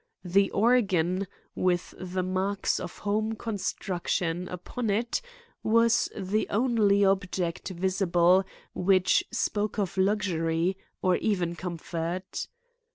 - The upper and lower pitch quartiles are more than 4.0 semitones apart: No, narrow, 2.6 semitones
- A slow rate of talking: Yes, slow, 100 wpm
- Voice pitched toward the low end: No, high, 190 Hz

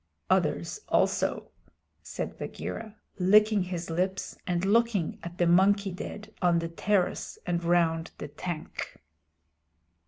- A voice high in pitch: No, medium, 180 Hz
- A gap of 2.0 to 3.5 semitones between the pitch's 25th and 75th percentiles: Yes, average, 2.9 semitones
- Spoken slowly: Yes, slow, 120 wpm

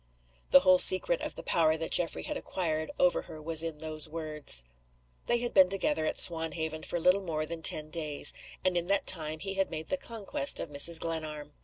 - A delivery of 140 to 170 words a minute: No, fast, 205 wpm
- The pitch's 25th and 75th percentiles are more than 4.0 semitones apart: No, average, 2.9 semitones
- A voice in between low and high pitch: Yes, medium, 165 Hz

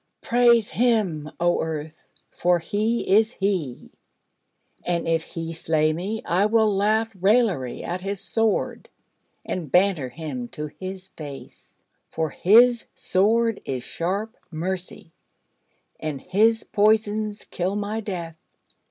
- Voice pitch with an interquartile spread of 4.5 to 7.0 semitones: Yes, average, 4.9 semitones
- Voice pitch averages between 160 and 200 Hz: Yes, high, 190 Hz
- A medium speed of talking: No, slow, 120 wpm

